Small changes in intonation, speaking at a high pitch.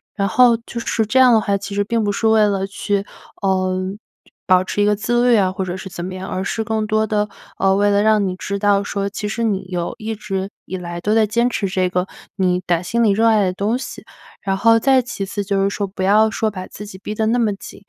Yes: narrow, 2.3 semitones; high, 205 Hz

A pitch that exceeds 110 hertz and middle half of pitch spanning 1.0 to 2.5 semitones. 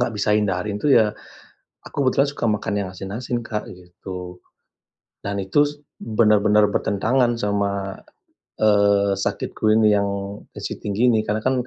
No: low, 105 Hz; narrow, 2.2 semitones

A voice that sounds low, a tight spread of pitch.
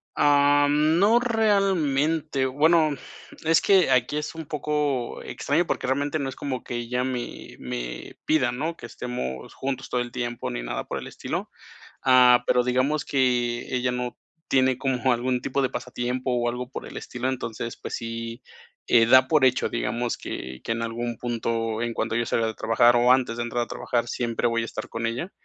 No: low, 125 Hz; average, 3.1 semitones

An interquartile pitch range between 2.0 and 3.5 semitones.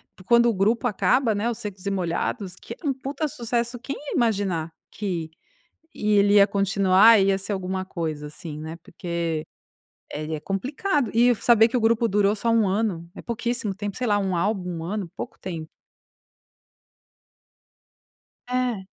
No: average, 4.2 semitones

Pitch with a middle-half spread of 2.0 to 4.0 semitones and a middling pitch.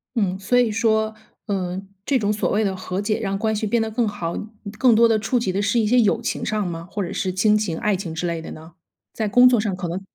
No: average, 3.1 semitones; high, 210 Hz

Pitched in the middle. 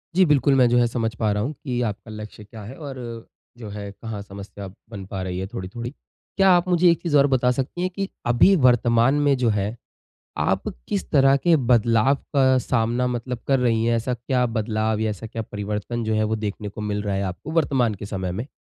No: low, 115 Hz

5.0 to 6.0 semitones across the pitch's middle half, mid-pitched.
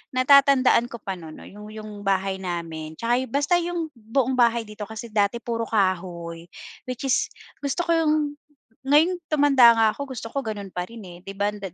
No: wide, 5.4 semitones; high, 225 Hz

